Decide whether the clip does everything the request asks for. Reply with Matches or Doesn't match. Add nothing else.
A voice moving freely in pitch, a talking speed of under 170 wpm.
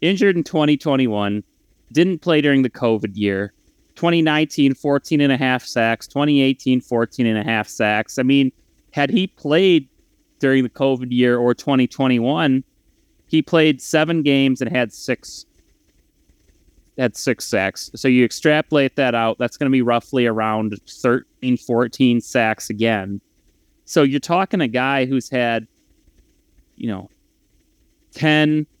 Doesn't match